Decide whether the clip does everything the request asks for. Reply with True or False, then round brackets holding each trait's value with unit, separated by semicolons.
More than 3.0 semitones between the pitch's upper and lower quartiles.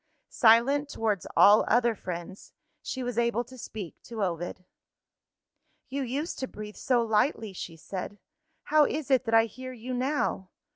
True (3.8 semitones)